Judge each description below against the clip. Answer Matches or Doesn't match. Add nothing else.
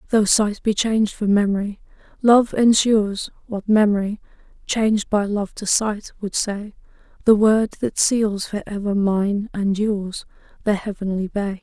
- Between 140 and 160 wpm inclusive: Matches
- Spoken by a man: Doesn't match